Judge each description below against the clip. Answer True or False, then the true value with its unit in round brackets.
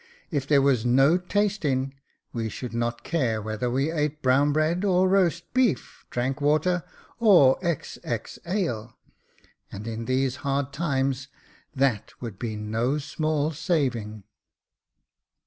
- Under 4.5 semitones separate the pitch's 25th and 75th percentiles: False (4.8 semitones)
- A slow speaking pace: True (130 wpm)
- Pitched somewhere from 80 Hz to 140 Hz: True (135 Hz)